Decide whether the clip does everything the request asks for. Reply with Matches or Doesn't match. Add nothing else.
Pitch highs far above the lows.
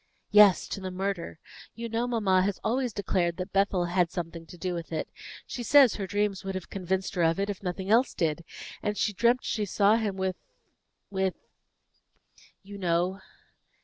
Doesn't match